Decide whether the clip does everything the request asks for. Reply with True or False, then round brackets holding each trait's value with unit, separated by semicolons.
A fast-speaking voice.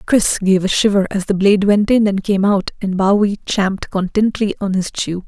True (215 wpm)